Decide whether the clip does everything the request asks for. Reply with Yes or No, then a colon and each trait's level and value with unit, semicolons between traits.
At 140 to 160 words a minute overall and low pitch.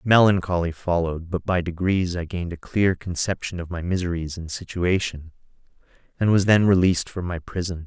No: average, 170 wpm; very low, 90 Hz